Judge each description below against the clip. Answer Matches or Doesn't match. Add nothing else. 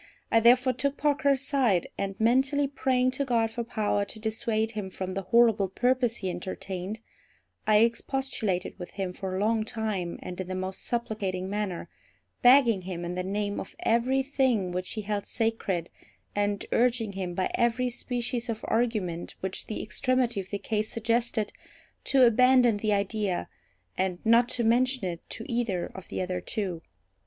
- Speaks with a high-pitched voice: Matches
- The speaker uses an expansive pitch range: Doesn't match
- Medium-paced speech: Matches